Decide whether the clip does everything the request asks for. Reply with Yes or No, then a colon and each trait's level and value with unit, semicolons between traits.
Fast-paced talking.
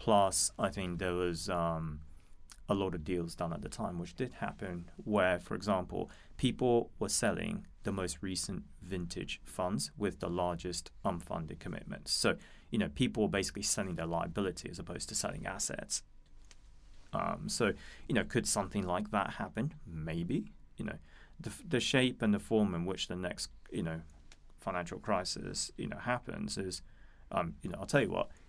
No: average, 175 wpm